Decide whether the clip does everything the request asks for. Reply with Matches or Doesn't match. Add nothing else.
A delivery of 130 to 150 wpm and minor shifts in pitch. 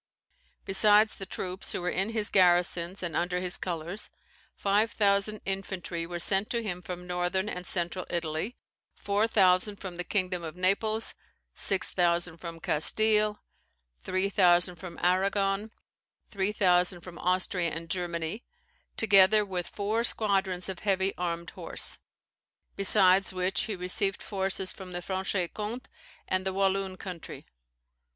Matches